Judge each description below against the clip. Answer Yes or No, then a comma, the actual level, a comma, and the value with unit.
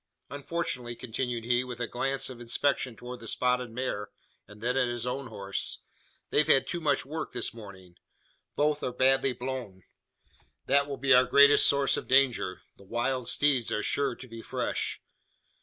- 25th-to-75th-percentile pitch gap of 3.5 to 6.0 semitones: No, average, 2.7 semitones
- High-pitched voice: No, low, 125 Hz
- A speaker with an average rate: Yes, average, 175 wpm